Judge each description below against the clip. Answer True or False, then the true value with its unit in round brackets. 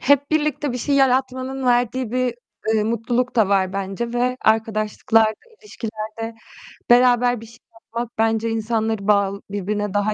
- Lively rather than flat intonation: False (2.7 semitones)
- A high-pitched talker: True (230 Hz)